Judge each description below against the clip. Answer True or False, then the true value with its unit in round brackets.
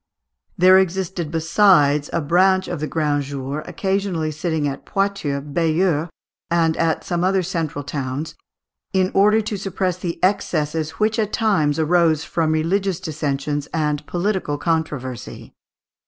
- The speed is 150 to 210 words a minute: False (135 wpm)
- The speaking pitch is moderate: True (165 Hz)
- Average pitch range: True (4.0 semitones)